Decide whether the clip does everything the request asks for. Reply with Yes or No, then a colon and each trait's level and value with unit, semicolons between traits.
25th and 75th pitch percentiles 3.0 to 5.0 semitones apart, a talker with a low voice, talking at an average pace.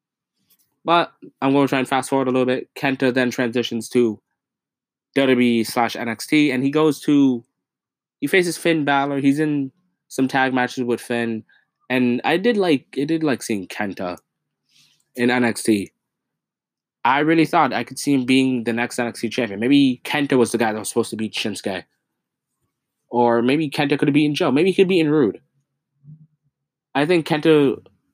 Yes: average, 3.5 semitones; low, 130 Hz; average, 175 wpm